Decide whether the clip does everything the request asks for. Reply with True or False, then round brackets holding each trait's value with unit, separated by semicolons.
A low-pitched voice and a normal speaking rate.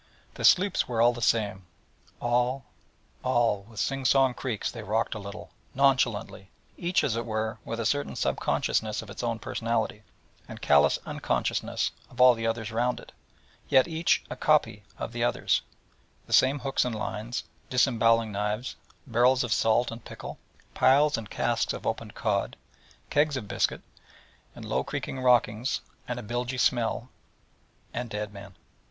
True (120 Hz; 160 wpm)